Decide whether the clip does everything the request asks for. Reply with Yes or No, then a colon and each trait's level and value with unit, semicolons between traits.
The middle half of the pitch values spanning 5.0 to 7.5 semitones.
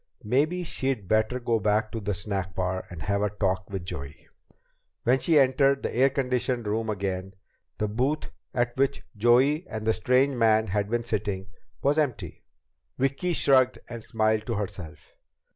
No: average, 4.3 semitones